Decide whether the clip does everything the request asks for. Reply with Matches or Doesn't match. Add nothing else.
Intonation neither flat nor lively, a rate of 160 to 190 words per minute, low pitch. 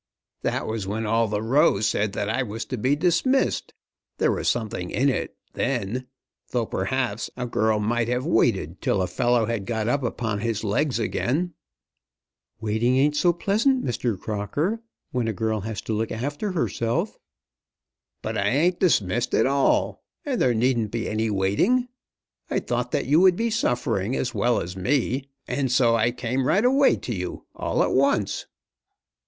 Matches